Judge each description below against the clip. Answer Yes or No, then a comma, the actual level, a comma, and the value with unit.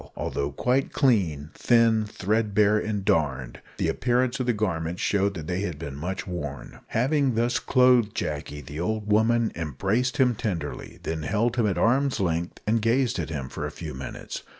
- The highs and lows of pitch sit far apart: Yes, wide, 6.4 semitones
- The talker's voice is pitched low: Yes, low, 105 Hz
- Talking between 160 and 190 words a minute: Yes, average, 175 wpm